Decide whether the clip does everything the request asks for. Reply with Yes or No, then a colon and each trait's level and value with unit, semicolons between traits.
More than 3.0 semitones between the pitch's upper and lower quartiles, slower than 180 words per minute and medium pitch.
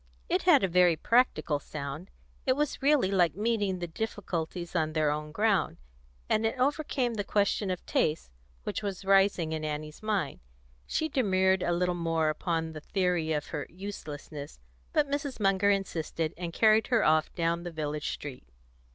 Yes: average, 4.7 semitones; average, 170 wpm; medium, 180 Hz